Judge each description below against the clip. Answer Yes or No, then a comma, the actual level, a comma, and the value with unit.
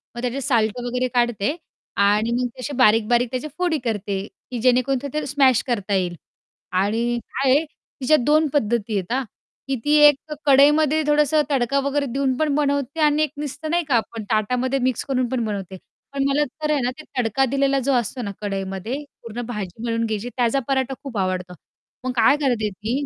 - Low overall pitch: No, very high, 250 Hz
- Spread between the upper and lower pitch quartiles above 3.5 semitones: Yes, average, 4.0 semitones